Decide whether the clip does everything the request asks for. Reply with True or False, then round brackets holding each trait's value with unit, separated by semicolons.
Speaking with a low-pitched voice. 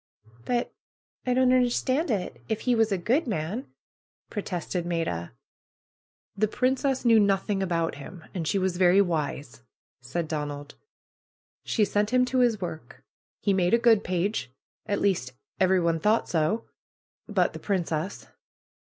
False (195 Hz)